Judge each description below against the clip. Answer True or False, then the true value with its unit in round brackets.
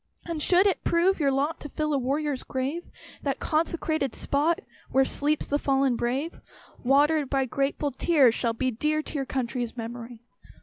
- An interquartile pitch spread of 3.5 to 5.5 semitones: False (3.0 semitones)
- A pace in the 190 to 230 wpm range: False (170 wpm)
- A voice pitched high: True (280 Hz)